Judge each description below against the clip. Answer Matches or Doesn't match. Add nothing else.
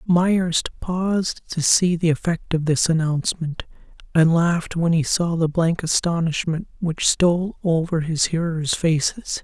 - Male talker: Matches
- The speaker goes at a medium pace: Matches